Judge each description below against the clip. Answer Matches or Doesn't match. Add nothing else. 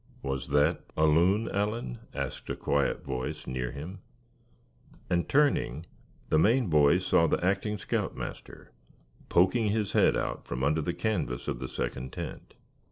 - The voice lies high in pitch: Doesn't match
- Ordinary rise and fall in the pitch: Doesn't match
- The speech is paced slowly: Doesn't match